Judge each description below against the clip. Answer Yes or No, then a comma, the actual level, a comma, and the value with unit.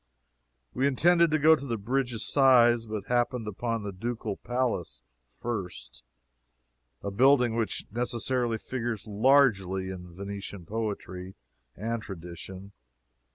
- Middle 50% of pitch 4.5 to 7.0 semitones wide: No, average, 4.1 semitones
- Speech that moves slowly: Yes, slow, 120 wpm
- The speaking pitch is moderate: No, low, 115 Hz